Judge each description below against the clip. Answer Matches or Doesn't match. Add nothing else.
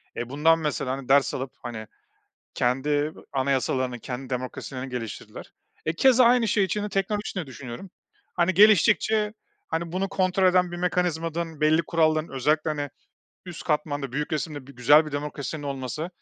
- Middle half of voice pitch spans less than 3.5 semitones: Doesn't match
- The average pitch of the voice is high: Doesn't match